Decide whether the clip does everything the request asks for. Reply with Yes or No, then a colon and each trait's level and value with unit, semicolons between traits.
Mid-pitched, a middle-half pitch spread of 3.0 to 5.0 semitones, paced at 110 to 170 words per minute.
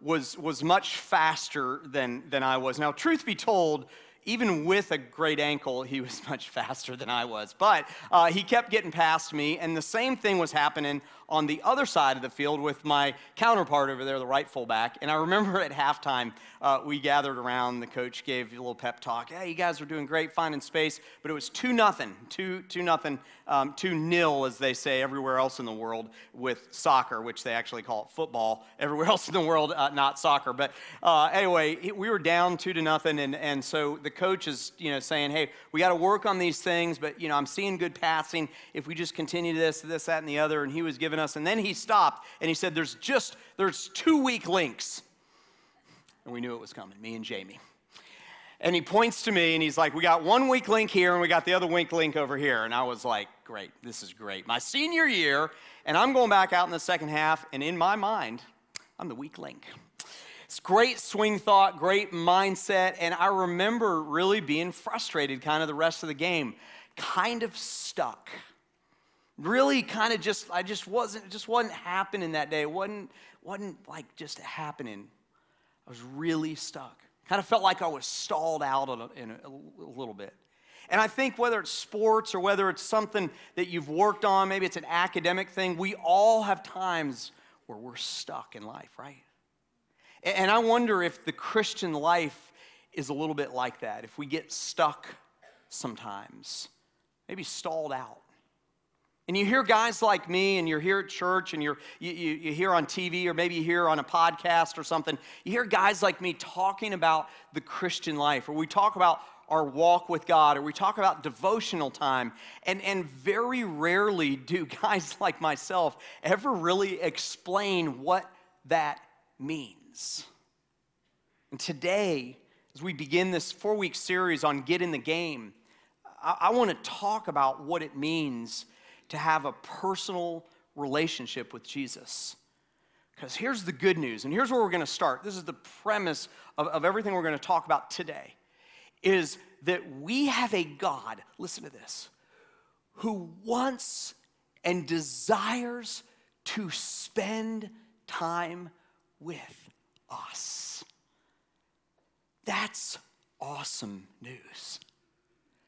No: medium, 170 Hz; average, 4.7 semitones; average, 185 wpm